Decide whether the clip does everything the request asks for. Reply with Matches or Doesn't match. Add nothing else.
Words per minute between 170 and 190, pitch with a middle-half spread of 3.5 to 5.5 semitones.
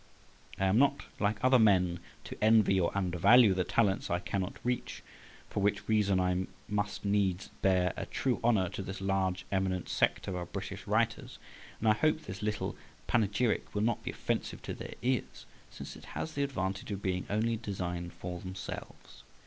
Doesn't match